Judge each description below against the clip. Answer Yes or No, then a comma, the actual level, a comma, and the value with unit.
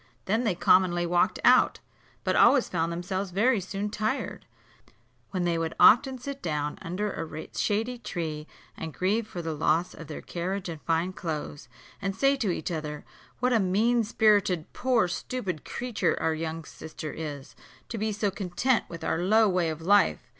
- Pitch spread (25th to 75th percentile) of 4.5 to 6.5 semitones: Yes, average, 4.9 semitones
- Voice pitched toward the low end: No, medium, 185 Hz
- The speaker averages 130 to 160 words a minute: No, average, 175 wpm